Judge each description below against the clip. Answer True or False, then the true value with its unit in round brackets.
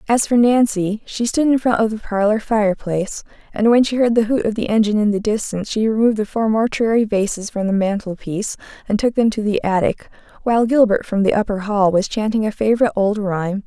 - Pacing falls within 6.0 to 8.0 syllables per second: True (6.1 syllables/s)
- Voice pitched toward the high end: True (215 Hz)